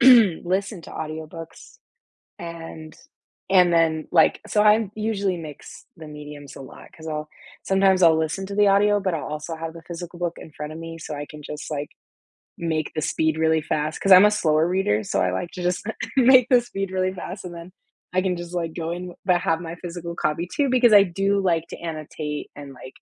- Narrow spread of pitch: No, average, 3.4 semitones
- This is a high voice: No, medium, 170 Hz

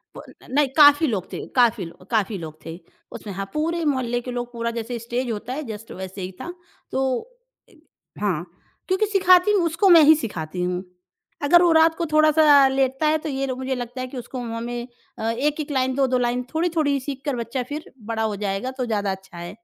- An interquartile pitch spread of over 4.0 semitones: Yes, average, 5.3 semitones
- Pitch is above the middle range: Yes, very high, 255 Hz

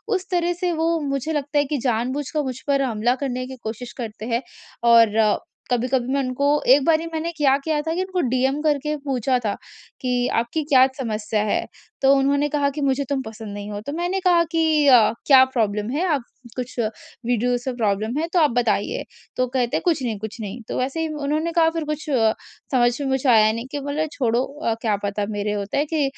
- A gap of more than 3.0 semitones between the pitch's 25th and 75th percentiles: Yes, average, 4.3 semitones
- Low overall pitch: No, very high, 260 Hz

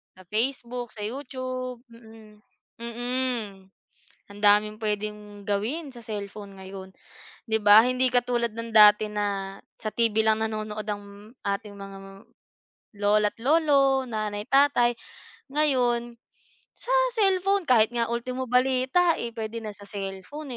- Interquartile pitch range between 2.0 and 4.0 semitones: Yes, average, 3.4 semitones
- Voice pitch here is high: Yes, high, 225 Hz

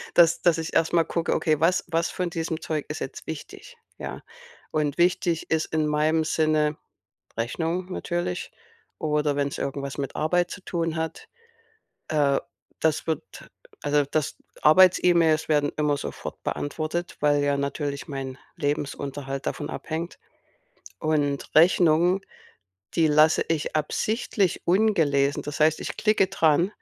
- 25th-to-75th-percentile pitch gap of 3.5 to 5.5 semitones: No, narrow, 2.6 semitones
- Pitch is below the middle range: No, medium, 155 Hz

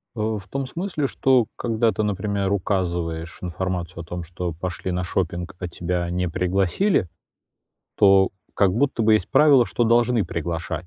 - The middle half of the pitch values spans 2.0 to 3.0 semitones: No, average, 4.2 semitones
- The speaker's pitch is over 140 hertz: No, very low, 95 Hz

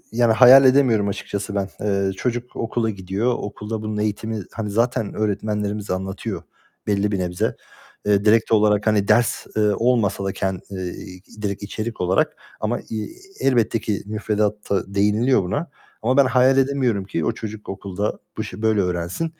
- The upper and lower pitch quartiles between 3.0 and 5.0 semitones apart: No, narrow, 2.5 semitones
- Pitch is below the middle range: Yes, low, 105 Hz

